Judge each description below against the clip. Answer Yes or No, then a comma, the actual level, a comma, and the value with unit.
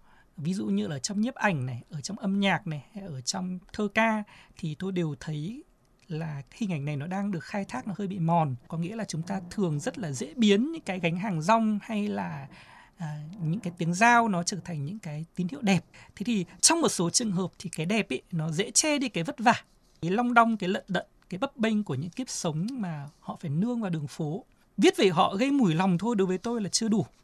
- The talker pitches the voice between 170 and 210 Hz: Yes, high, 190 Hz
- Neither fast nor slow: No, fast, 255 wpm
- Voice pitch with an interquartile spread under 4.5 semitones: No, average, 4.8 semitones